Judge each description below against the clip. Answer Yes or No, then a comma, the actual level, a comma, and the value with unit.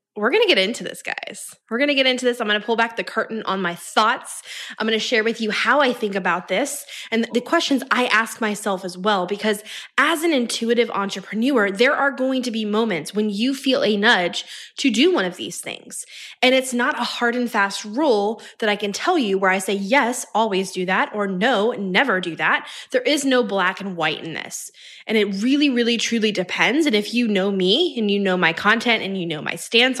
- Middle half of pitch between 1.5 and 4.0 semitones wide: No, average, 4.4 semitones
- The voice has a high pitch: Yes, high, 225 Hz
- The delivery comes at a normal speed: No, fast, 235 wpm